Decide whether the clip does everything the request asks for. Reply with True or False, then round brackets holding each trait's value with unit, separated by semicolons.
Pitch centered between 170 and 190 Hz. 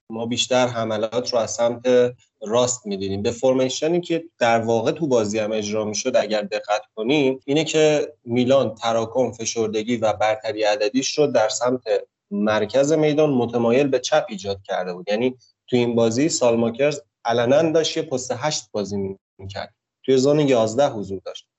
False (120 Hz)